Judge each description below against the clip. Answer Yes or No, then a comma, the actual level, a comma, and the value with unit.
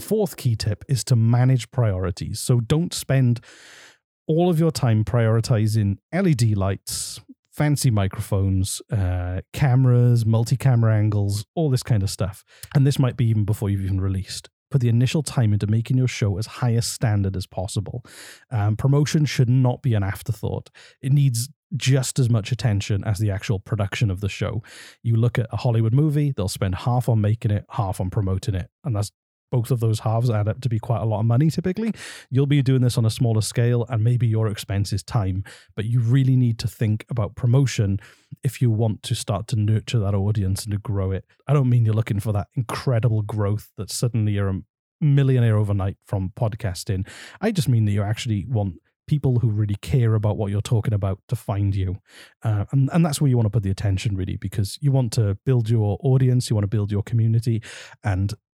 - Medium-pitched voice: No, low, 115 Hz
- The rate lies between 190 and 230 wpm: Yes, fast, 205 wpm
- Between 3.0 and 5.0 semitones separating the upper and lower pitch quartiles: Yes, average, 3.7 semitones